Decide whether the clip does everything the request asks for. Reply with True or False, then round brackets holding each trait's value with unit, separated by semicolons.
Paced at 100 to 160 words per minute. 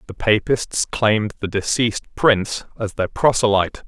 True (140 wpm)